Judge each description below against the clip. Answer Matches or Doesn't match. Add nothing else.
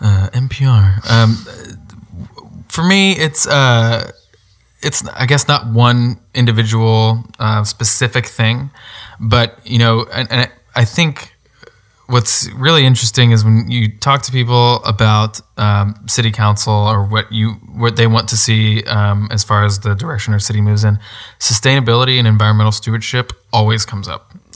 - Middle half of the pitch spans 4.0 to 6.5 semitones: Doesn't match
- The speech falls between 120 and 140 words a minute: Doesn't match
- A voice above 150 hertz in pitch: Doesn't match